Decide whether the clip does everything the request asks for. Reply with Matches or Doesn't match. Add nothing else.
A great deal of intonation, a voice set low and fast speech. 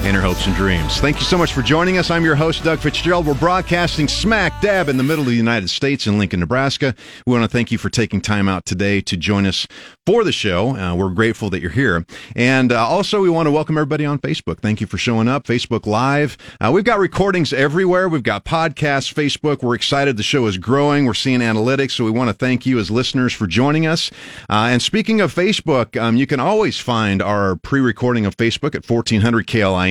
Matches